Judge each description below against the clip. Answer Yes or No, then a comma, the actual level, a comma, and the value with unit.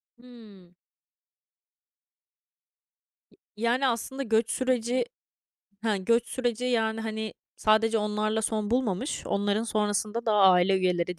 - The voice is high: Yes, high, 220 Hz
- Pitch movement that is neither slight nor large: No, narrow, 2.3 semitones